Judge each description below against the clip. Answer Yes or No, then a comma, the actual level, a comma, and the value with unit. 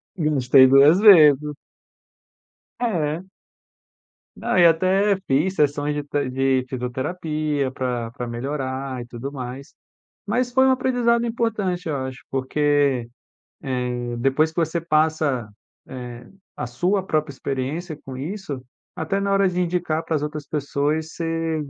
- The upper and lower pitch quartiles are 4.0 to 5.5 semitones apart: Yes, average, 4.8 semitones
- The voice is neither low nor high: Yes, medium, 150 Hz